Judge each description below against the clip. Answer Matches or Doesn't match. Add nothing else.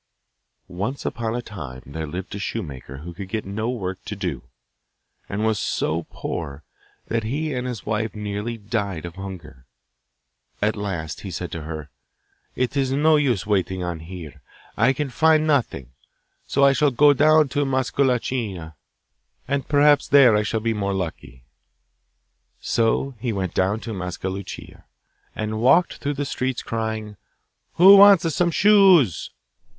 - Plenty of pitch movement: Matches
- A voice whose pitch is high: Doesn't match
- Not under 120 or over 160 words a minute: Matches